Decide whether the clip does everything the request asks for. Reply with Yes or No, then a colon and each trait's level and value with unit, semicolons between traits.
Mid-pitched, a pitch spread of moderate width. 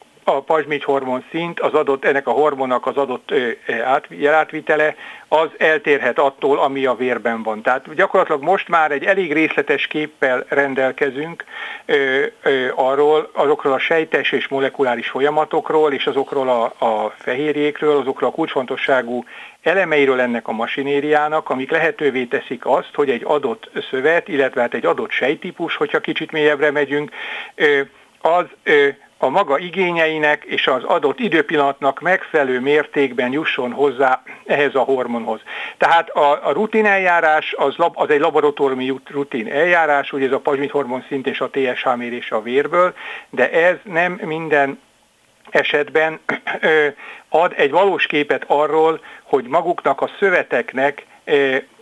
Yes: medium, 150 Hz; average, 3.5 semitones